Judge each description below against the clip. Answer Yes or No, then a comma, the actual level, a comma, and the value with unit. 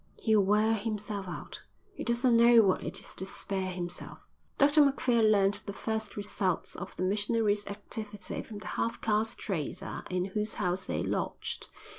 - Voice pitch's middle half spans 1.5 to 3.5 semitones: Yes, narrow, 2.5 semitones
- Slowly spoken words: No, average, 165 wpm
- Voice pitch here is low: No, high, 210 Hz